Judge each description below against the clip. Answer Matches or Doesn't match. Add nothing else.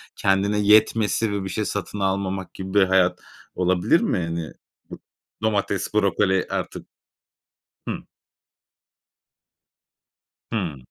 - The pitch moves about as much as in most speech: Doesn't match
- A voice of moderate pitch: Doesn't match